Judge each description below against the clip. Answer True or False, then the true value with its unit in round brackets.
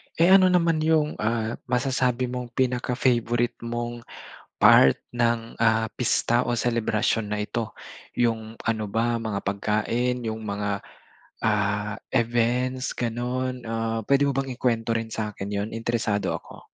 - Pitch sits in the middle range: False (115 Hz)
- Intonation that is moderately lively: False (2.1 semitones)